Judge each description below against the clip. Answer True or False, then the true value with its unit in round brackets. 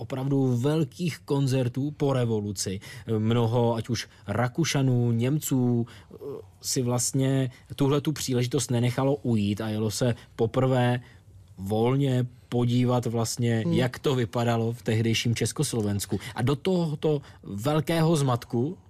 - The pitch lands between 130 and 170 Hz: False (120 Hz)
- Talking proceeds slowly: True (110 wpm)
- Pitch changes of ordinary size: True (3.0 semitones)